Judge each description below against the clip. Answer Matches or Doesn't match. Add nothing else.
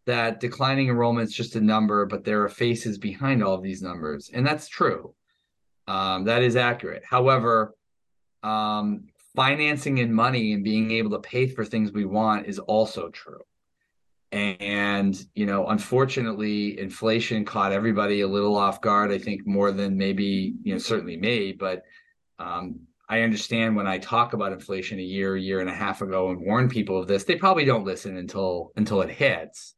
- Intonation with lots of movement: Doesn't match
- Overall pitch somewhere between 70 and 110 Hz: Matches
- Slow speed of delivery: Doesn't match